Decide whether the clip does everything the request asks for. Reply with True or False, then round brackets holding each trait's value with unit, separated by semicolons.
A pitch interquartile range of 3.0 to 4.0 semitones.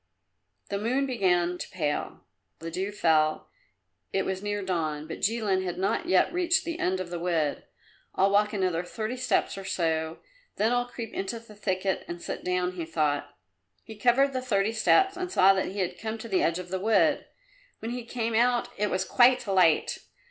False (4.6 semitones)